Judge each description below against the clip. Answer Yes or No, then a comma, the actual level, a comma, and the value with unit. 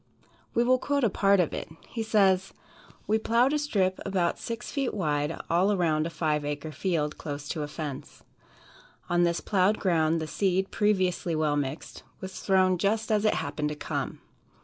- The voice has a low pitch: No, medium, 185 Hz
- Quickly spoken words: No, average, 180 wpm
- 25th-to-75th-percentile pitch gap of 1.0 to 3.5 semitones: No, average, 5.0 semitones